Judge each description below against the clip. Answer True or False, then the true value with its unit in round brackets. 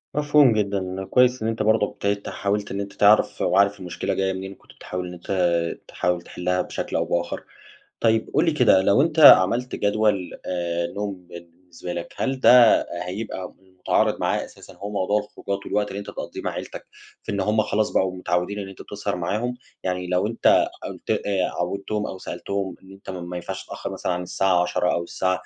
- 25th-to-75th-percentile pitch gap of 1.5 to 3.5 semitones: True (2.6 semitones)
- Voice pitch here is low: True (100 Hz)